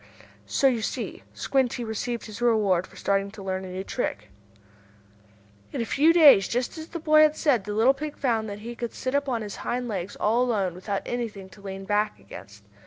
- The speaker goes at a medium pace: No, fast, 210 wpm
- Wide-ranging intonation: No, average, 4.2 semitones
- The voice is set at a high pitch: Yes, high, 225 Hz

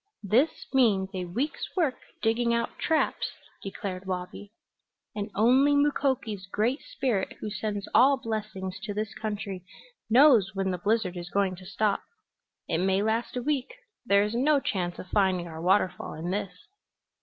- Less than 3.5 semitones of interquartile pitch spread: No, average, 4.2 semitones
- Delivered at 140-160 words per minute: Yes, average, 155 wpm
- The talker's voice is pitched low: No, high, 210 Hz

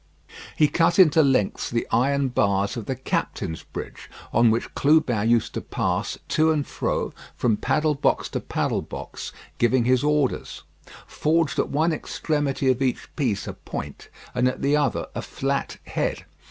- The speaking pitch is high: No, low, 135 Hz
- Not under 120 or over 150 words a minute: No, average, 165 wpm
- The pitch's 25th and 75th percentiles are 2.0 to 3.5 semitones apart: No, average, 4.0 semitones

